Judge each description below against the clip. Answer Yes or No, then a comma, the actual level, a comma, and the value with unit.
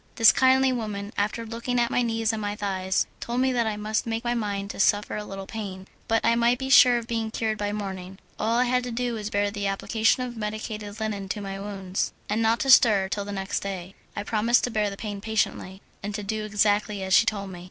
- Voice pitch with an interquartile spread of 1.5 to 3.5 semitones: Yes, narrow, 2.4 semitones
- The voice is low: No, high, 215 Hz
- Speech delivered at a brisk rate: Yes, fast, 250 wpm